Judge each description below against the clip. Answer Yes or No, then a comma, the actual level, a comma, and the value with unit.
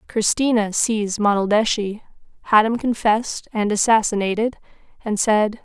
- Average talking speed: No, slow, 105 wpm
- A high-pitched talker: Yes, high, 215 Hz